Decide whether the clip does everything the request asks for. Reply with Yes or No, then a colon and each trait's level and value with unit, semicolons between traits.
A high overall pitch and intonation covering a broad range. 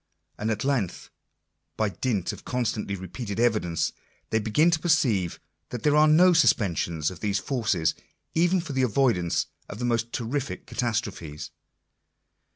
No: low, 115 Hz; wide, 5.8 semitones